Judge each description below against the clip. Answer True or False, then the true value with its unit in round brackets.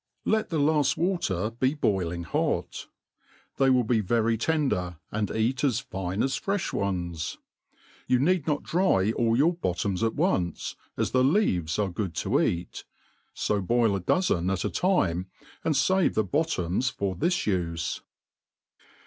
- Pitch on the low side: True (115 Hz)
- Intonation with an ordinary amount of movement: False (8.0 semitones)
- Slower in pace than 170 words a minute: True (150 wpm)